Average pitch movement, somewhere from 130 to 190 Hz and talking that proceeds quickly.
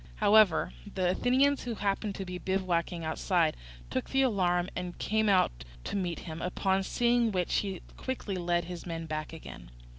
No: average, 3.2 semitones; medium, 185 Hz; average, 170 wpm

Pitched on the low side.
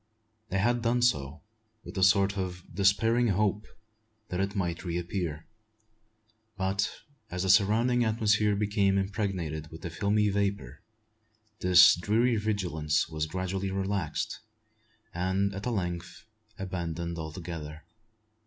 Yes: very low, 95 Hz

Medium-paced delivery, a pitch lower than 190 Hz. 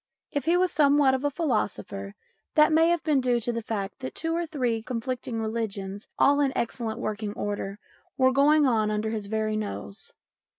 No: average, 185 wpm; high, 240 Hz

